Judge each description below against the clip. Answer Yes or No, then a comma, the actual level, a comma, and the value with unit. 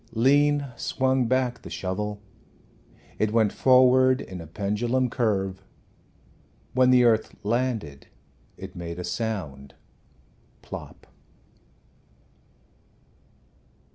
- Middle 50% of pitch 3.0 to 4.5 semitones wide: No, average, 5.0 semitones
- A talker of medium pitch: No, low, 115 Hz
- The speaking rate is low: Yes, slow, 90 wpm